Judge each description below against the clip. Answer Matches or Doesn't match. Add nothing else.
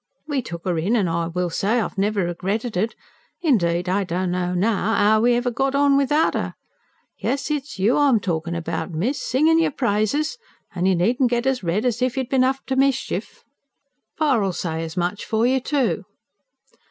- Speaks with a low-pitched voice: Doesn't match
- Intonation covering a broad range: Matches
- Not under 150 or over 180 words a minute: Doesn't match